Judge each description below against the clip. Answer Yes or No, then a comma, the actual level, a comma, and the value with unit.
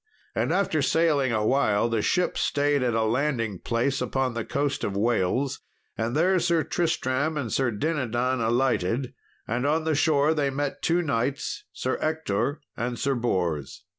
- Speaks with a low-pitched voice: Yes, low, 130 Hz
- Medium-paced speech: Yes, average, 160 wpm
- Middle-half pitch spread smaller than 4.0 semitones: No, average, 4.3 semitones